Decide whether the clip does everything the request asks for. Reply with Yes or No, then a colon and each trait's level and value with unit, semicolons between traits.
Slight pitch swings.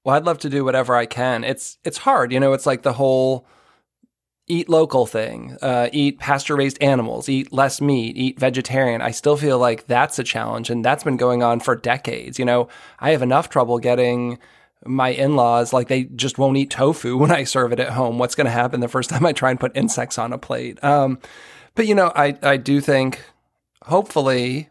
Yes: narrow, 2.3 semitones